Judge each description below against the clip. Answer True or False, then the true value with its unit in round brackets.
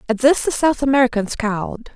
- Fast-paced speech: False (185 wpm)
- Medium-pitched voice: False (250 Hz)